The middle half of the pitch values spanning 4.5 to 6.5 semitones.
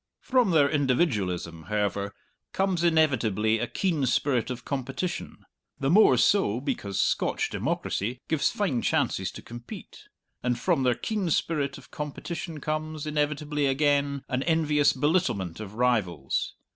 Yes: average, 4.9 semitones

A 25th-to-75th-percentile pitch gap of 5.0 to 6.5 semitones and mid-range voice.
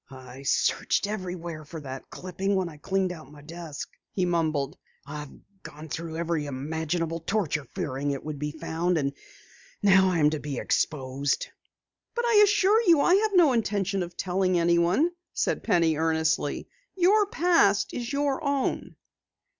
Yes: average, 5.3 semitones; medium, 170 Hz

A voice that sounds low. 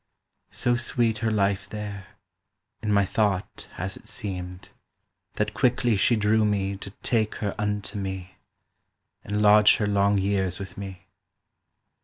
Yes: low, 100 Hz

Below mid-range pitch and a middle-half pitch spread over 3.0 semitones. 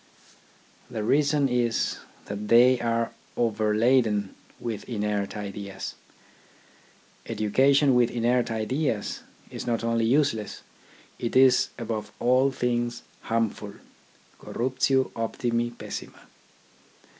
No: low, 115 Hz; average, 2.7 semitones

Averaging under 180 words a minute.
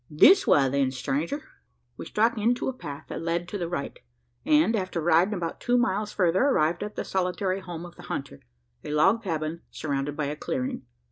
No: average, 195 wpm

